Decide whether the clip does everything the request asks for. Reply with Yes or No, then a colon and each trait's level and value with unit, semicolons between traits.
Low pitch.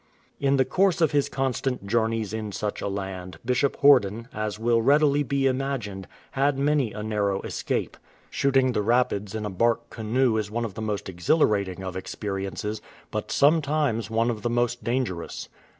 Yes: low, 115 Hz